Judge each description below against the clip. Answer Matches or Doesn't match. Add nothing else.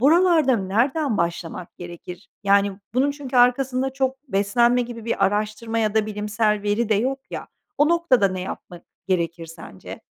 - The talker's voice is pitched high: Matches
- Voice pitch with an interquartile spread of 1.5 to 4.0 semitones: Doesn't match